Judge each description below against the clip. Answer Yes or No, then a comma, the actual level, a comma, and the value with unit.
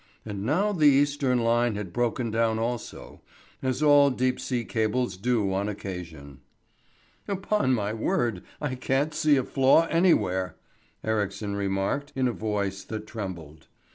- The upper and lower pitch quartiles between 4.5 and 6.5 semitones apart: Yes, average, 5.0 semitones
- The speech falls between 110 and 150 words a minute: Yes, average, 140 wpm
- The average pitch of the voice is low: Yes, low, 115 Hz